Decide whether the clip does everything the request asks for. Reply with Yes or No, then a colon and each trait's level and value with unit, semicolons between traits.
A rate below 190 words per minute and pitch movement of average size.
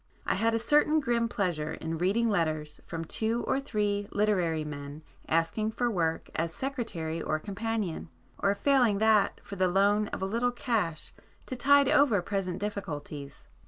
No: average, 160 wpm; wide, 5.8 semitones